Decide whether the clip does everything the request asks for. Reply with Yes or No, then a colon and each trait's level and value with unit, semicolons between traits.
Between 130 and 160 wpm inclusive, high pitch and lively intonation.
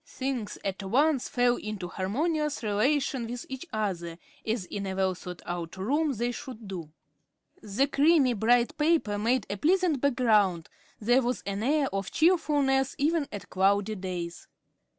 Yes: average, 150 wpm; high, 235 Hz; wide, 5.9 semitones